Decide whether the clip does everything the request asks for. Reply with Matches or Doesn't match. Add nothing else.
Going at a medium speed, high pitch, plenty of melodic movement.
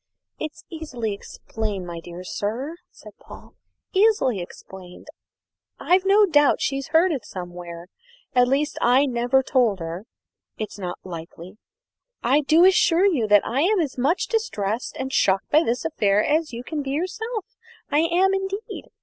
Matches